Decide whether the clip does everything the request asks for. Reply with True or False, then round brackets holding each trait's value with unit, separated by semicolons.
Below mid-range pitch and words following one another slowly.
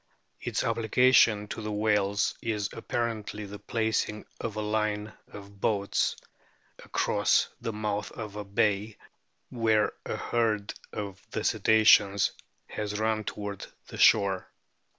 True (105 Hz; 130 wpm)